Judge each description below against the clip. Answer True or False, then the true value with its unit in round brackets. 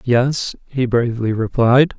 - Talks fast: False (120 wpm)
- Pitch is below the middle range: True (125 Hz)